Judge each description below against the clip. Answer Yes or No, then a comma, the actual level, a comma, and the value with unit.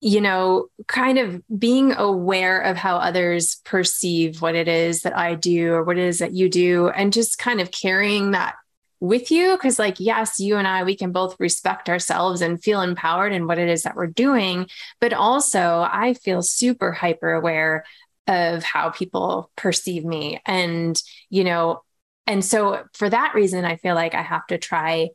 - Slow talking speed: No, average, 190 wpm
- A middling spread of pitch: Yes, average, 3.5 semitones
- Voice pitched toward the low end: No, medium, 185 Hz